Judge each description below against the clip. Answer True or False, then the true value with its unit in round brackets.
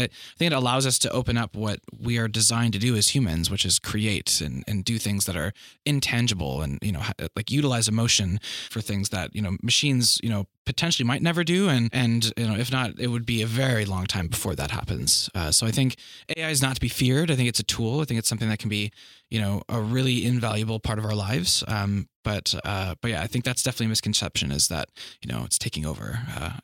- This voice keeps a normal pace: False (250 wpm)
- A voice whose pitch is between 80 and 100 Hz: False (110 Hz)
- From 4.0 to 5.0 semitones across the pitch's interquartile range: False (3.6 semitones)